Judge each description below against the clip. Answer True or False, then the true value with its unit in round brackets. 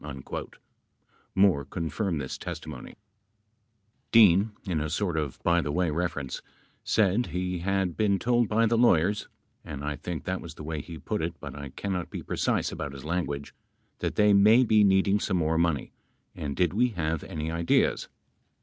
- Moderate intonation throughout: True (4.6 semitones)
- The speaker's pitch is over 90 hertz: False (85 Hz)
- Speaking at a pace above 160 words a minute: True (180 wpm)